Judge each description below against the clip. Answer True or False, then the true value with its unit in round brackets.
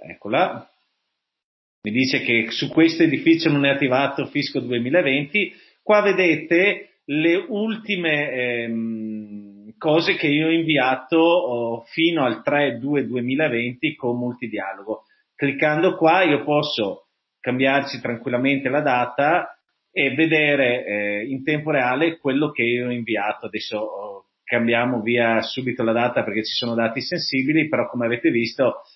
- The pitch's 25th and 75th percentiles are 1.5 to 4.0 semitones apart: False (5.0 semitones)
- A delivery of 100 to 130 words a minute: True (125 wpm)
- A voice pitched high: False (140 Hz)